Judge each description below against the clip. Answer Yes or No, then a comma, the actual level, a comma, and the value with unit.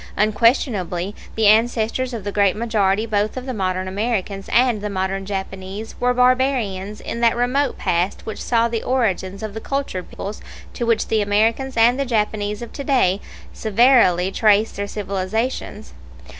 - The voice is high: Yes, high, 215 Hz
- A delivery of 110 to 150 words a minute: No, average, 160 wpm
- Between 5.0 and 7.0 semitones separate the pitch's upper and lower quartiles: No, average, 3.4 semitones